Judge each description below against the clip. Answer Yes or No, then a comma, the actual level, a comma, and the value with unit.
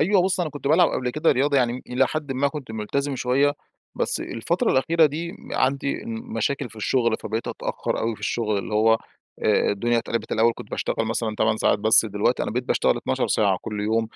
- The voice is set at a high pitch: No, low, 125 Hz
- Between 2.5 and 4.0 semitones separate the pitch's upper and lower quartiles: No, average, 4.4 semitones